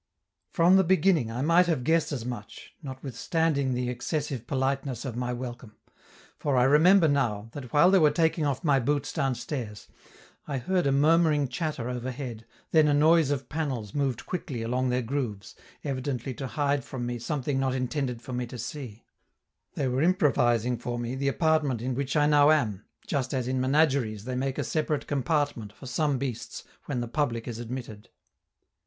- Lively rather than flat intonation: No, average, 3.4 semitones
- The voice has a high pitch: No, low, 135 Hz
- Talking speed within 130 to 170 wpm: No, average, 180 wpm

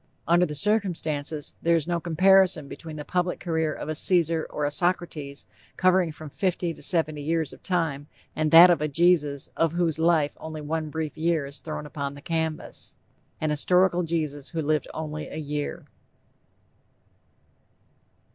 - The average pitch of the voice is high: No, medium, 160 Hz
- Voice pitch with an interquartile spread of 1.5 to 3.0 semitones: Yes, narrow, 2.5 semitones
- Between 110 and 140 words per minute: No, average, 165 wpm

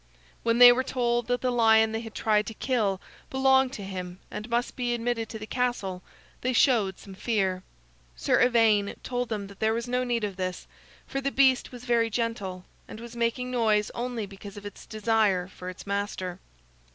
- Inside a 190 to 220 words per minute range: Yes, average, 195 wpm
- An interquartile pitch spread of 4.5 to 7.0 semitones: No, average, 3.3 semitones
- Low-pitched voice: No, high, 225 Hz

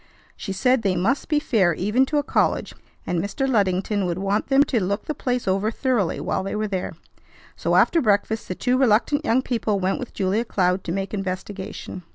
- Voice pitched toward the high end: Yes, high, 205 Hz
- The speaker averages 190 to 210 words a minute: Yes, fast, 205 wpm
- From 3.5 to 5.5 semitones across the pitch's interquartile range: Yes, average, 4.8 semitones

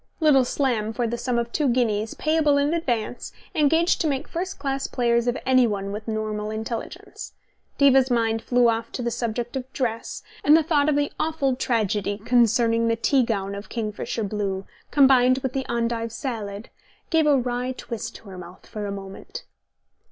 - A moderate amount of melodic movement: Yes, average, 3.7 semitones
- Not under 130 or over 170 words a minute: No, average, 180 wpm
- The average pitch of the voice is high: Yes, high, 240 Hz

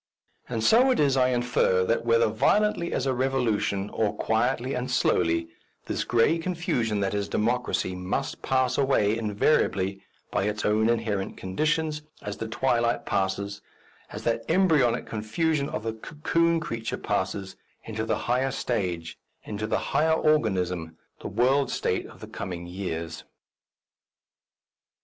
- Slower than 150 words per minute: Yes, average, 140 wpm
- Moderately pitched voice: No, low, 115 Hz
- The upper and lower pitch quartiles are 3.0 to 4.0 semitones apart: No, average, 5.0 semitones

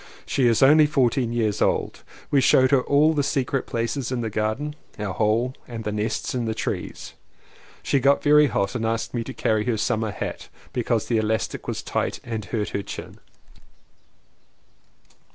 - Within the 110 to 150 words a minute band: No, average, 180 wpm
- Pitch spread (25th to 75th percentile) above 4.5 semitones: No, average, 3.8 semitones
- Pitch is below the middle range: Yes, low, 120 Hz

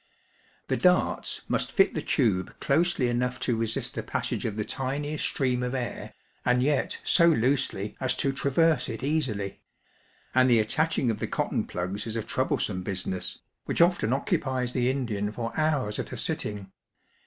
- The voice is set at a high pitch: No, low, 125 Hz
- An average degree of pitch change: Yes, average, 4.3 semitones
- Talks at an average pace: Yes, average, 165 wpm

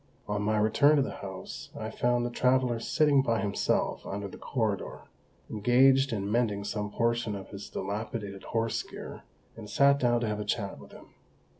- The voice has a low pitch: Yes, low, 115 Hz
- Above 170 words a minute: Yes, average, 180 wpm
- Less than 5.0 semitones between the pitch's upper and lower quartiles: Yes, average, 3.0 semitones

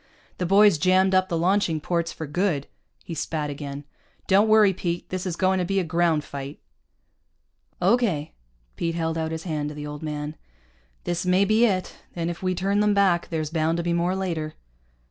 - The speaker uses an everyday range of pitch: Yes, average, 3.2 semitones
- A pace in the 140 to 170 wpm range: No, average, 195 wpm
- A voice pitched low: No, medium, 170 Hz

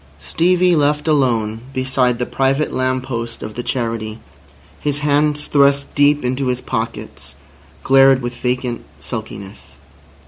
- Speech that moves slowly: Yes, slow, 130 wpm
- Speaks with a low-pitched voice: Yes, low, 130 Hz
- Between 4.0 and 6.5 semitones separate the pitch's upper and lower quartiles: No, average, 3.1 semitones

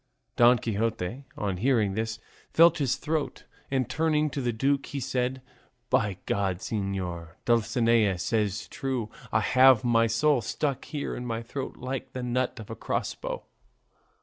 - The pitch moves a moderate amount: Yes, average, 3.8 semitones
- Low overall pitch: Yes, low, 120 Hz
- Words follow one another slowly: No, average, 150 wpm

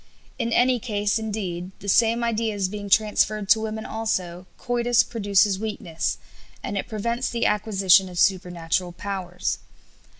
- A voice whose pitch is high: Yes, high, 205 Hz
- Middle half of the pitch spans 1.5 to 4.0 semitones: Yes, average, 3.1 semitones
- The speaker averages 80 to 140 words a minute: Yes, slow, 135 wpm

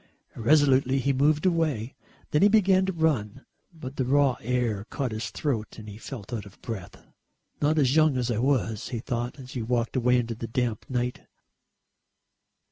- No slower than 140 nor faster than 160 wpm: No, average, 180 wpm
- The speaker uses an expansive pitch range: No, average, 3.9 semitones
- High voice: No, low, 125 Hz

